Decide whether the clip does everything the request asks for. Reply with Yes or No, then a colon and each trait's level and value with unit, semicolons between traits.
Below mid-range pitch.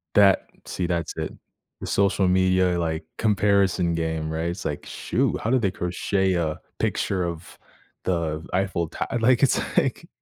Yes: very low, 90 Hz